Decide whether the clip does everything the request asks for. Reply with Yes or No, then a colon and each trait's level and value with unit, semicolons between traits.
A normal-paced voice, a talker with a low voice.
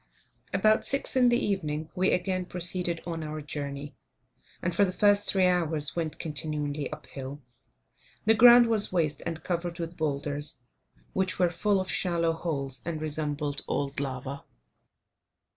No: average, 150 wpm; medium, 165 Hz